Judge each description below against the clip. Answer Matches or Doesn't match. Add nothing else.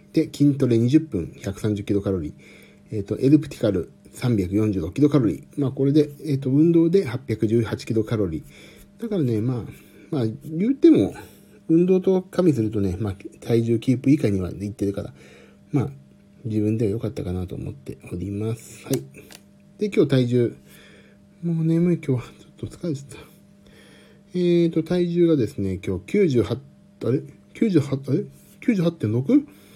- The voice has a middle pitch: Doesn't match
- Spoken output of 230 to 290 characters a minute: Matches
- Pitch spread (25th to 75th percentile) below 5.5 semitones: Doesn't match